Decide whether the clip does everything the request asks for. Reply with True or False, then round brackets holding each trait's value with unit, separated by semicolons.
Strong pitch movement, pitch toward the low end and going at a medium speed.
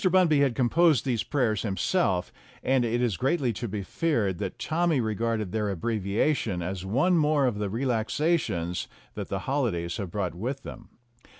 True (6.2 semitones; 115 Hz; 165 wpm)